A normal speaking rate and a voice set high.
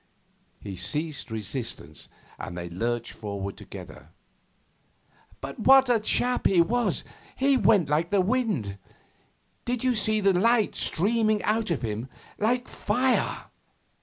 No: slow, 130 wpm; high, 195 Hz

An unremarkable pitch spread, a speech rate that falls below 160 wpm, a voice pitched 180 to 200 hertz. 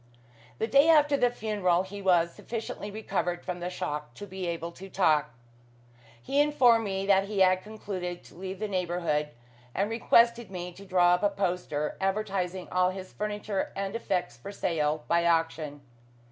No: average, 3.0 semitones; average, 170 wpm; high, 190 Hz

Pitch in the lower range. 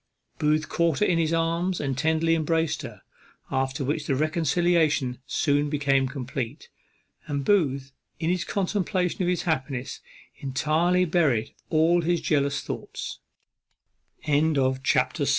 No: medium, 155 Hz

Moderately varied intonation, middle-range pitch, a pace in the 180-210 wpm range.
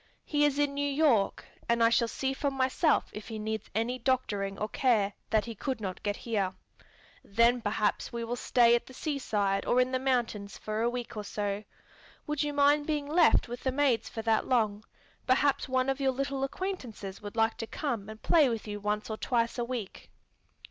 No: average, 4.0 semitones; high, 235 Hz; fast, 205 wpm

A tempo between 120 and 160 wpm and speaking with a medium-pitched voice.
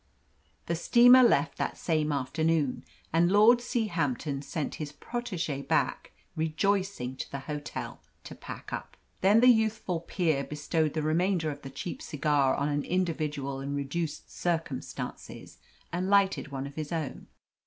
Yes: average, 145 wpm; medium, 160 Hz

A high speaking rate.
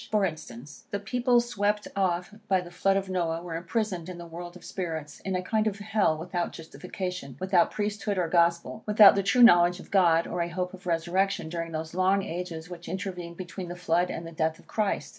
Yes: fast, 215 wpm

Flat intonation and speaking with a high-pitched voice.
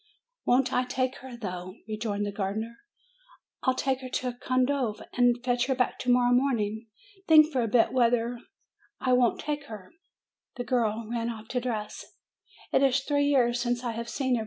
Yes: narrow, 2.2 semitones; high, 245 Hz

